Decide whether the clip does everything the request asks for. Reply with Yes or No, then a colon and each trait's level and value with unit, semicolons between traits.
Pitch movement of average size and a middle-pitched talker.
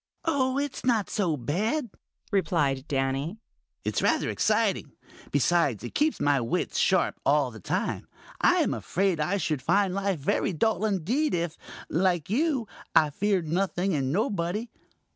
No: wide, 6.2 semitones; medium, 180 Hz